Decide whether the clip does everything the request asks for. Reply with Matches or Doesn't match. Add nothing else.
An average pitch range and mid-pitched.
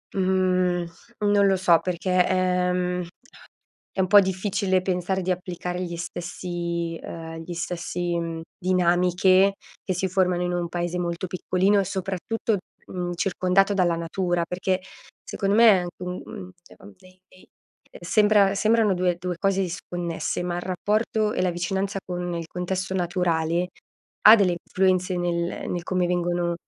Doesn't match